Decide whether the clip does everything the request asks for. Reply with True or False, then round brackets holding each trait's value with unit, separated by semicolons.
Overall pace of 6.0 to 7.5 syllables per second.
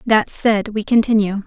False (4.4 syllables/s)